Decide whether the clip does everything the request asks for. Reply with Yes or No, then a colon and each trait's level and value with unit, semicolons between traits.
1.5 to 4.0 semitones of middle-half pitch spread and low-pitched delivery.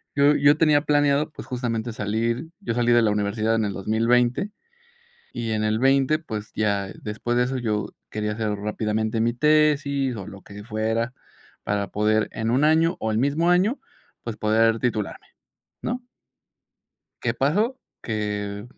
No: average, 4.8 semitones; low, 115 Hz